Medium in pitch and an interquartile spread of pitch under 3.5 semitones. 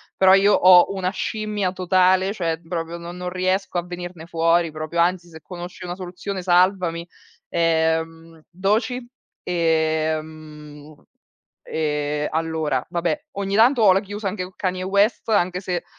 Yes: medium, 175 Hz; average, 2.7 semitones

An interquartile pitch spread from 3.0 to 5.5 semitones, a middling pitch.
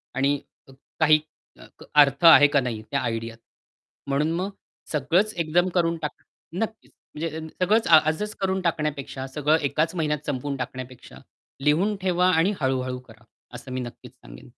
Yes: average, 4.7 semitones; medium, 150 Hz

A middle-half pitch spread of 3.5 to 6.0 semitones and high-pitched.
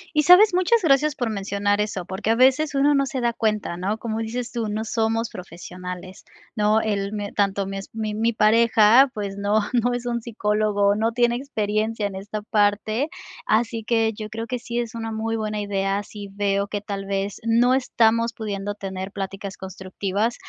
No: narrow, 2.6 semitones; high, 215 Hz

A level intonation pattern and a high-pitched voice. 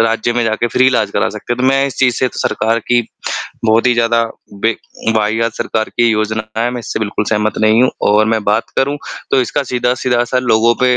No: narrow, 2.2 semitones; low, 115 Hz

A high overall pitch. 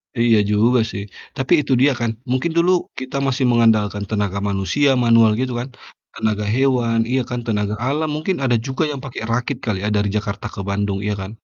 No: low, 115 Hz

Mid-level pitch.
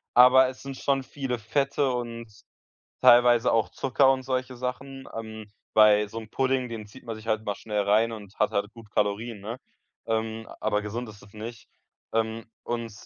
No: low, 115 Hz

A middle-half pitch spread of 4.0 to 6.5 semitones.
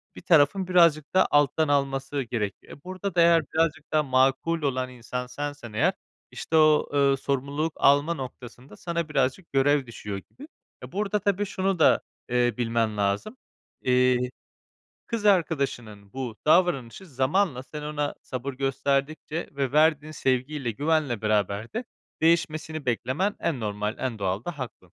Yes: average, 4.4 semitones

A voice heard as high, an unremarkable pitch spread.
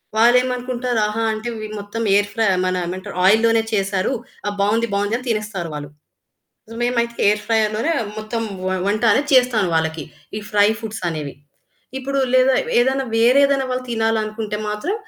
Yes: high, 220 Hz; average, 3.1 semitones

